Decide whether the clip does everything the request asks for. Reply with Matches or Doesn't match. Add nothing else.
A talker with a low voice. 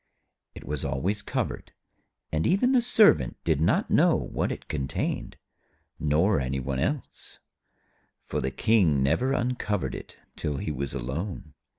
Matches